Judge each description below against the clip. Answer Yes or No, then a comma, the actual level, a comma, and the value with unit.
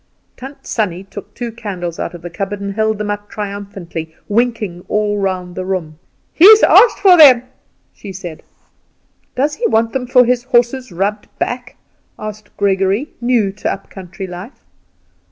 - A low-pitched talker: No, high, 205 Hz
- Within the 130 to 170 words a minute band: Yes, average, 160 wpm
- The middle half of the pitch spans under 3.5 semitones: No, average, 4.1 semitones